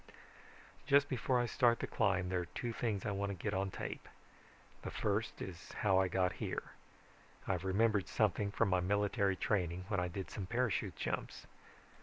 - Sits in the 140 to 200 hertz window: No, low, 100 Hz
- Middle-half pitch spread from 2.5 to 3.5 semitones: Yes, average, 2.9 semitones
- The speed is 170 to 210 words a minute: Yes, average, 180 wpm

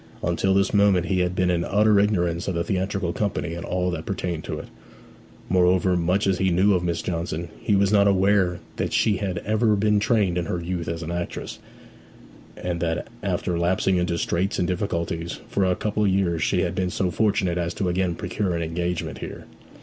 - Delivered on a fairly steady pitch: Yes, narrow, 2.3 semitones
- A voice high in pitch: No, very low, 90 Hz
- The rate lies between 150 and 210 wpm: Yes, fast, 205 wpm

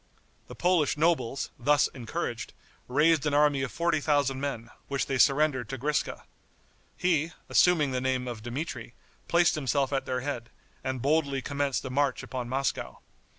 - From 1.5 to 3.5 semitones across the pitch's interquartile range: Yes, narrow, 2.6 semitones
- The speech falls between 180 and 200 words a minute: No, average, 155 wpm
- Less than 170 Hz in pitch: Yes, medium, 140 Hz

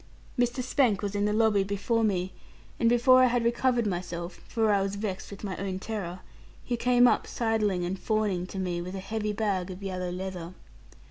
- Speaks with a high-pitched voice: Yes, high, 200 Hz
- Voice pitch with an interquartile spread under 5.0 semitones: Yes, average, 3.5 semitones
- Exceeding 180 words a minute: Yes, average, 200 wpm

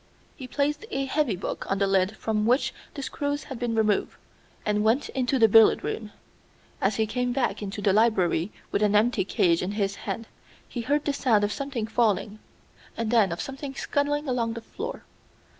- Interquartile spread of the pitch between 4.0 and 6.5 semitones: Yes, average, 4.4 semitones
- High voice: Yes, high, 225 Hz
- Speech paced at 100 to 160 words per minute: No, average, 190 wpm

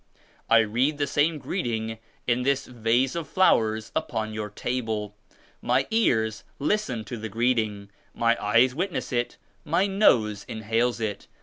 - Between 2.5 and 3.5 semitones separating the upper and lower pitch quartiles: No, average, 3.9 semitones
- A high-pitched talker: No, low, 120 Hz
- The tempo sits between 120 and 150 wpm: Yes, average, 145 wpm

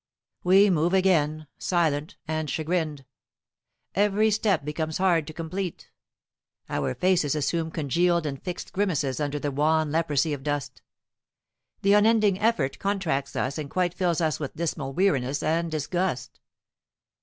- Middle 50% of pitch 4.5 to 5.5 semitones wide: No, average, 3.9 semitones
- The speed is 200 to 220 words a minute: No, slow, 135 wpm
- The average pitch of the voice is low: No, medium, 160 Hz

